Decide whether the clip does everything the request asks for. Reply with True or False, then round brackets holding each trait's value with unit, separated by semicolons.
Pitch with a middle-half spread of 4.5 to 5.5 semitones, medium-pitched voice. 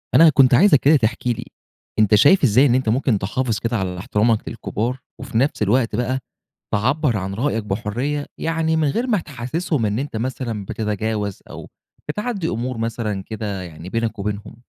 False (4.8 semitones; 120 Hz)